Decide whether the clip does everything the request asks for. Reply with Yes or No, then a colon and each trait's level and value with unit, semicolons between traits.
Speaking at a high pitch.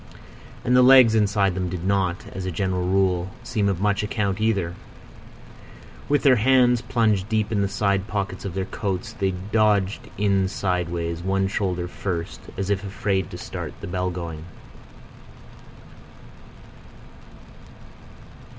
No: very low, 95 Hz